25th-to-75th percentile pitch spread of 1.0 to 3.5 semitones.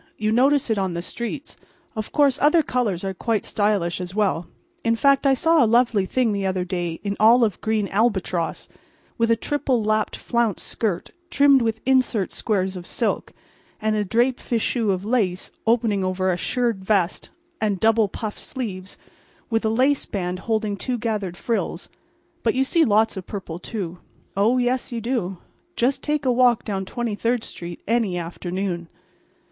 No: average, 4.2 semitones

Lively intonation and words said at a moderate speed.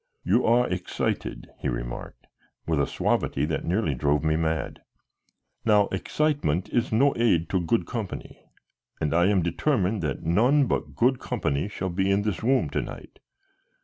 Yes: wide, 6.4 semitones; average, 160 wpm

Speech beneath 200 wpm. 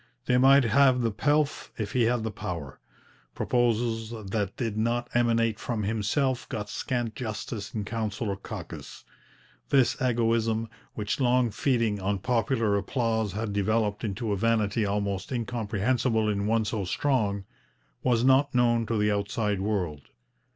Yes: average, 145 wpm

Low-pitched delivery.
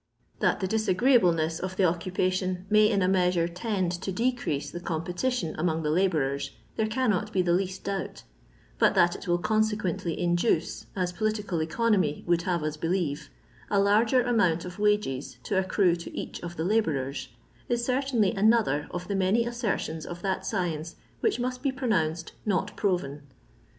No: medium, 185 Hz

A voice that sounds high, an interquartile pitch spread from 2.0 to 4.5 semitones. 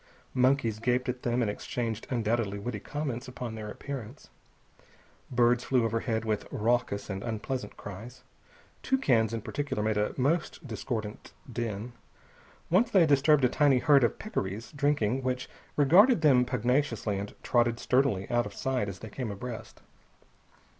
No: low, 120 Hz; average, 3.6 semitones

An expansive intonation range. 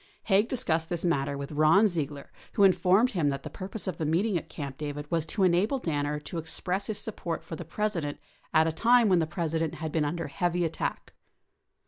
No: average, 4.1 semitones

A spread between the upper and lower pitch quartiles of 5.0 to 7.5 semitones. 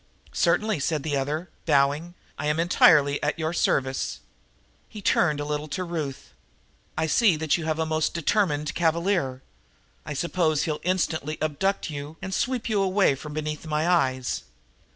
No: average, 3.1 semitones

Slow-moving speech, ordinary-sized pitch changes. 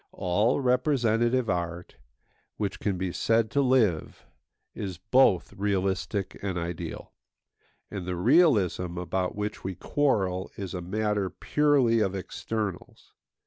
Yes: slow, 120 wpm; average, 4.2 semitones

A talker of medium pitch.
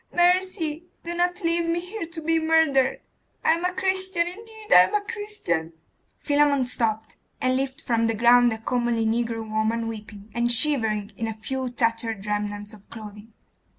No: very high, 250 Hz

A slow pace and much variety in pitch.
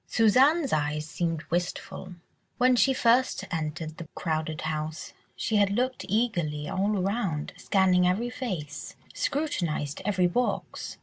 Yes: slow, 125 wpm; wide, 7.0 semitones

